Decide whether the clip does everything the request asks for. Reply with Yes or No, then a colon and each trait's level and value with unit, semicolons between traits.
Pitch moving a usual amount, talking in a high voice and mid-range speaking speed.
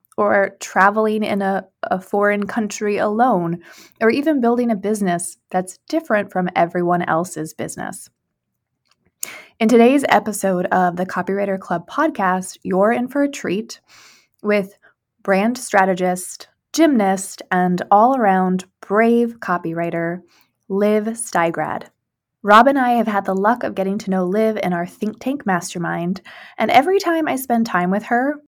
Yes: average, 3.8 semitones; high, 200 Hz; average, 145 wpm